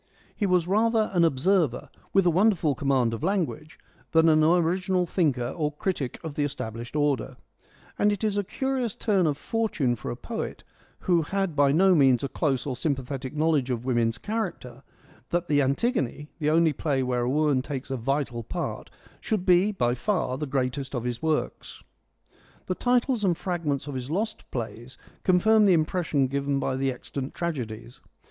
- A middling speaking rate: Yes, average, 180 wpm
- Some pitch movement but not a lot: No, wide, 5.7 semitones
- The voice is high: No, medium, 150 Hz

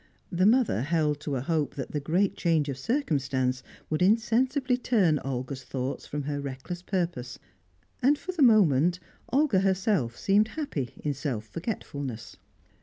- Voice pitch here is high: No, medium, 160 Hz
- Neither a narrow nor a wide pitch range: No, wide, 7.7 semitones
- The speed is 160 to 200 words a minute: No, average, 150 wpm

